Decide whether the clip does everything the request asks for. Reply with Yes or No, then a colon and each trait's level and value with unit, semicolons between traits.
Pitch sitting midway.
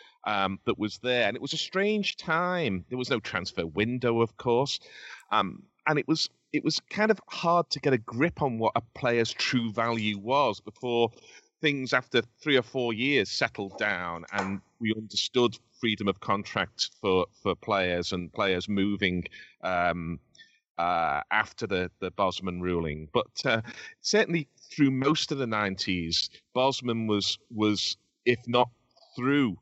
No: low, 115 Hz